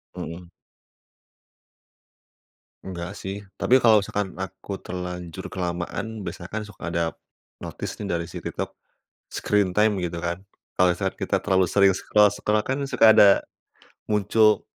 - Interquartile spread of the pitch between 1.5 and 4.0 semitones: Yes, average, 3.1 semitones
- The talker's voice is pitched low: Yes, very low, 95 Hz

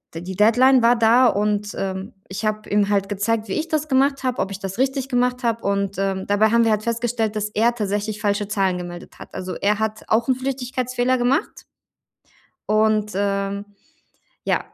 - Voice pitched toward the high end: Yes, high, 215 Hz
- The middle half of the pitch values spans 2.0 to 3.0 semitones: No, average, 3.4 semitones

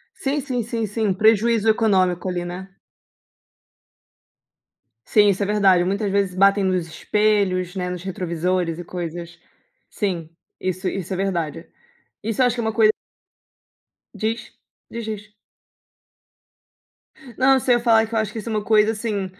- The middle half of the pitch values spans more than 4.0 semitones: No, average, 3.3 semitones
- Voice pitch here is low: No, high, 200 Hz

